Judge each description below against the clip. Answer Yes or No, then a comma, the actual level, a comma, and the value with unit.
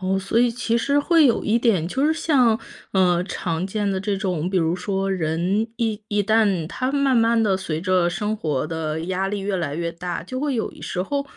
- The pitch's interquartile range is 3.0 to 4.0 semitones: No, average, 4.5 semitones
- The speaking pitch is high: Yes, high, 195 Hz